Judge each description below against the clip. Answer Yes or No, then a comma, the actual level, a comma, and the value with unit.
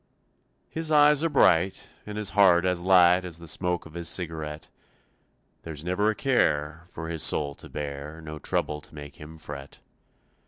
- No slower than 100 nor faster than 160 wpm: No, average, 170 wpm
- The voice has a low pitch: Yes, very low, 85 Hz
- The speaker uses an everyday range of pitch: Yes, average, 3.6 semitones